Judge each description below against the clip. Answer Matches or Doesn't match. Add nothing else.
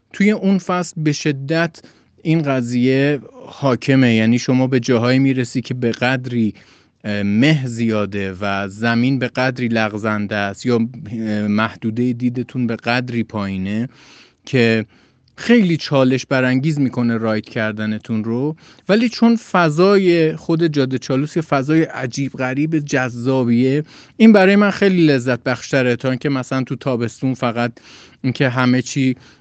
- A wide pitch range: Doesn't match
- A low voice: Matches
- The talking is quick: Doesn't match